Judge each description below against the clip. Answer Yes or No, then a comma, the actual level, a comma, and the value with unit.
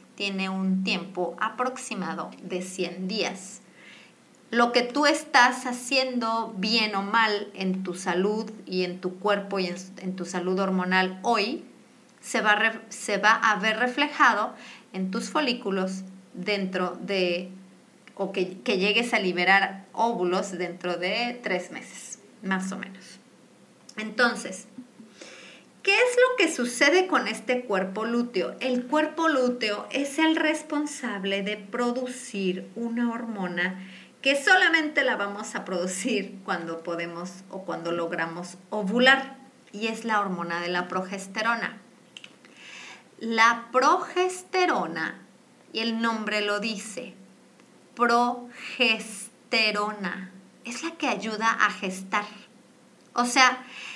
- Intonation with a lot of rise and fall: No, average, 4.5 semitones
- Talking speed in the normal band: No, slow, 120 wpm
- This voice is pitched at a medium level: No, high, 215 Hz